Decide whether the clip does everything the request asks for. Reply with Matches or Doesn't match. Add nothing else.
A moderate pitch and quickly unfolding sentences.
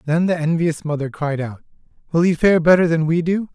Matches